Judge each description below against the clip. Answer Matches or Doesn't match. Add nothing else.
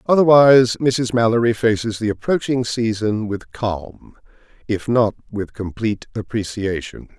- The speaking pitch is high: Doesn't match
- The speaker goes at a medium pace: Doesn't match